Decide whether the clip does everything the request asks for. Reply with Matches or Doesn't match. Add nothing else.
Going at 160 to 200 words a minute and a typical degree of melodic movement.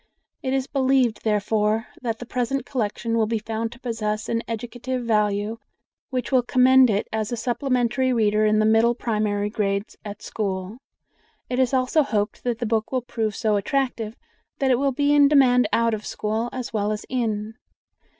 Matches